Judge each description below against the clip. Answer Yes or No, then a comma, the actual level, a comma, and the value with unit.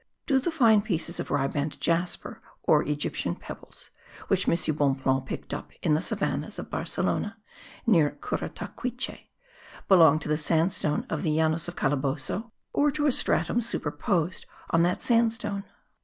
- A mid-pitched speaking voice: Yes, medium, 170 Hz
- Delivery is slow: No, average, 145 wpm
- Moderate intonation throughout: No, wide, 6.9 semitones